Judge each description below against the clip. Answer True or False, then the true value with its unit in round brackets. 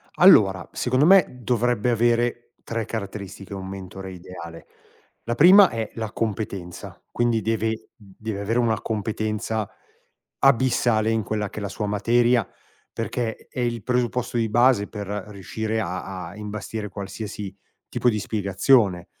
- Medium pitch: False (110 Hz)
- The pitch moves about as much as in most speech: True (3.0 semitones)